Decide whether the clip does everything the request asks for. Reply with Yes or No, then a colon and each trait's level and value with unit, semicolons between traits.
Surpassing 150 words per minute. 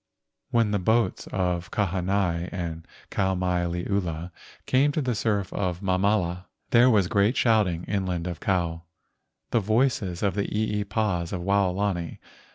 No: average, 140 wpm